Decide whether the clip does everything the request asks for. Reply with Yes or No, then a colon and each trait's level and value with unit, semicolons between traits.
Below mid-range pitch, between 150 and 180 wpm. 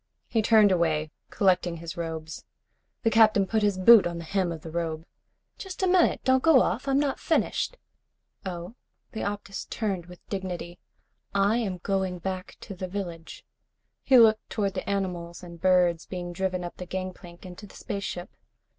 No: medium, 185 Hz; average, 170 wpm